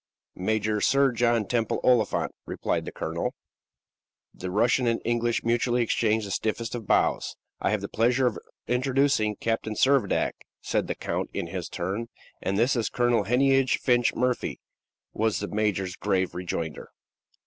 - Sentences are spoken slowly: No, average, 155 wpm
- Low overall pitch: Yes, low, 115 Hz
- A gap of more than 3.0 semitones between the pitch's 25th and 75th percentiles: No, average, 2.7 semitones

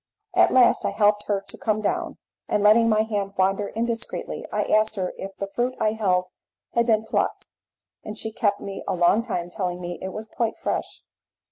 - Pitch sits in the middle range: No, high, 210 Hz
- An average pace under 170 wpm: No, average, 200 wpm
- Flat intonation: Yes, narrow, 2.3 semitones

